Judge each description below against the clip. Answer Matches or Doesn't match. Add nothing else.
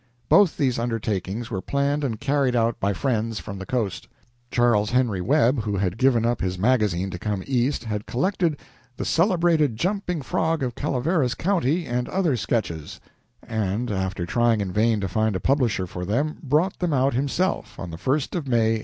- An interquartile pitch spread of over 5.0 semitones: Matches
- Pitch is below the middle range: Matches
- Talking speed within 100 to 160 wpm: Doesn't match